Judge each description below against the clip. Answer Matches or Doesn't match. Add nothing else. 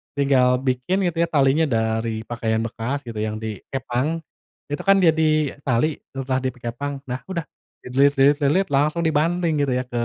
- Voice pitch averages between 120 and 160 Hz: Matches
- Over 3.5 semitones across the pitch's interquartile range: Matches